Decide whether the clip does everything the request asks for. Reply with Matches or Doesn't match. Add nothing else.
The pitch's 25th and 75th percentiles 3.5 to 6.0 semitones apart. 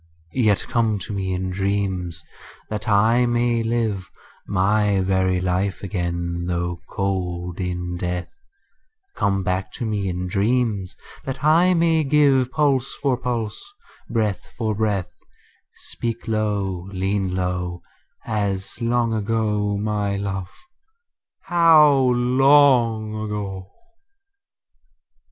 Matches